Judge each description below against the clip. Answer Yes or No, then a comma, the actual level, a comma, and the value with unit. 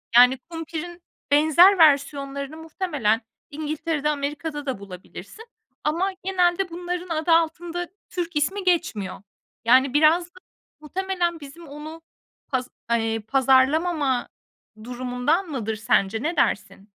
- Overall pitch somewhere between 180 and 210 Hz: No, very high, 305 Hz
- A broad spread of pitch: No, average, 4.8 semitones